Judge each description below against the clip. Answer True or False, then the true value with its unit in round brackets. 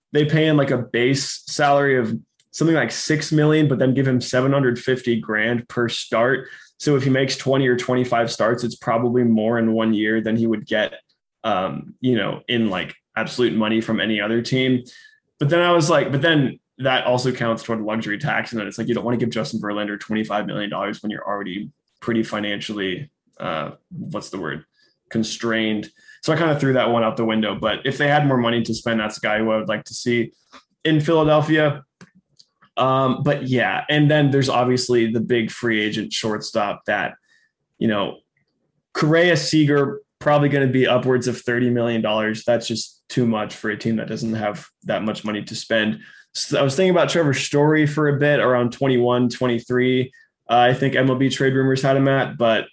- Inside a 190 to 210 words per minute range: True (205 wpm)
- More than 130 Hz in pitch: False (125 Hz)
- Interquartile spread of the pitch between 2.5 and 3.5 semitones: False (3.9 semitones)